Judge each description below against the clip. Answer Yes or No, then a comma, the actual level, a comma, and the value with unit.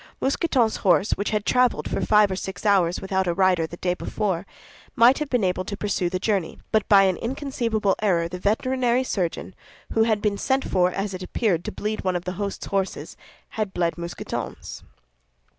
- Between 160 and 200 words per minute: Yes, average, 195 wpm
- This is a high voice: Yes, high, 200 Hz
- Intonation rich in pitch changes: No, average, 3.3 semitones